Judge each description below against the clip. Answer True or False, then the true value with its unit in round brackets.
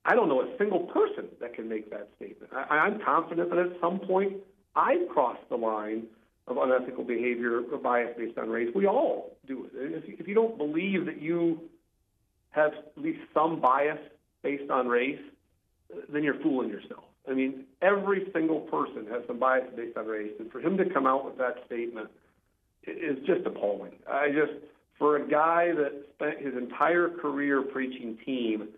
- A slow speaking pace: False (180 wpm)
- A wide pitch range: True (6.2 semitones)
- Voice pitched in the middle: True (145 Hz)